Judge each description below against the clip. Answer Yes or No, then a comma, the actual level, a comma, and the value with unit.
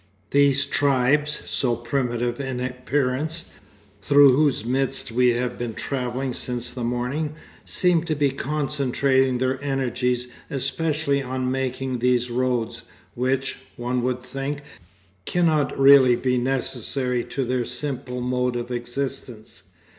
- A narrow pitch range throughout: Yes, narrow, 2.1 semitones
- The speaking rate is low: Yes, slow, 125 wpm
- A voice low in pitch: Yes, low, 130 Hz